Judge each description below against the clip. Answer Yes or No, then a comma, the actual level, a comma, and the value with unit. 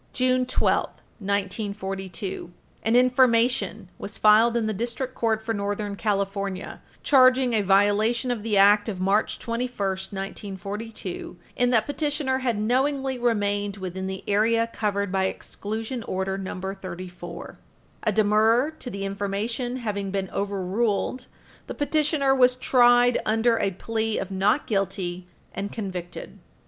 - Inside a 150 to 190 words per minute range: No, slow, 135 wpm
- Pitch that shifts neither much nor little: Yes, average, 3.7 semitones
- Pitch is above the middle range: Yes, high, 210 Hz